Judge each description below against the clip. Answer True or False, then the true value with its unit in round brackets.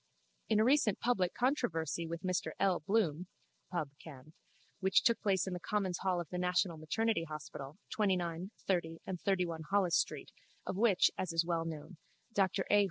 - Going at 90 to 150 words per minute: False (170 wpm)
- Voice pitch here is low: False (180 Hz)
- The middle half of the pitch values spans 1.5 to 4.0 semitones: True (3.2 semitones)